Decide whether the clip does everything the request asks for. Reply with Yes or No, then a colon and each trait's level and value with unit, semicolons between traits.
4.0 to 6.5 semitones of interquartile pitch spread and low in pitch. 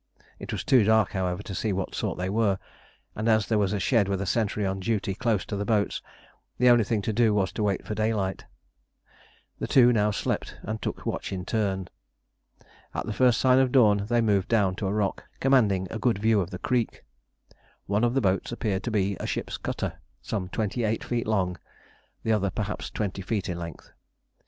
No: average, 2.7 semitones; low, 105 Hz